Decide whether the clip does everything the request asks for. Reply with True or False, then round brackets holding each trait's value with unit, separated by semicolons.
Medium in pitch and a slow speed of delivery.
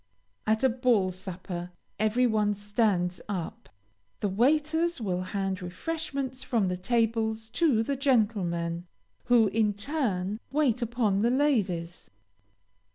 False (220 Hz; 120 wpm)